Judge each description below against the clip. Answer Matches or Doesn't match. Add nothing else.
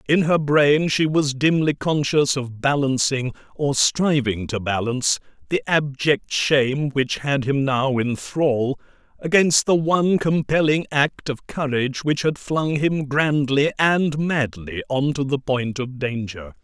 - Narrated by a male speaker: Matches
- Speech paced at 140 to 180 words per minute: Matches